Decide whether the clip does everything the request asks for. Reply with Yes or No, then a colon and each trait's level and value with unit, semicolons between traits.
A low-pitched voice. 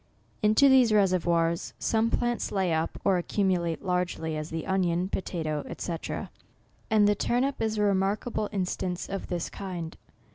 No: high, 190 Hz